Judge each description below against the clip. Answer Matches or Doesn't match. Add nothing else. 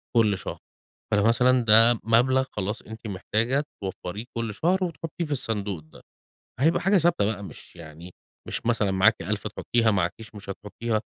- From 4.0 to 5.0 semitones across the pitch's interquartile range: Doesn't match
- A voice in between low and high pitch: Doesn't match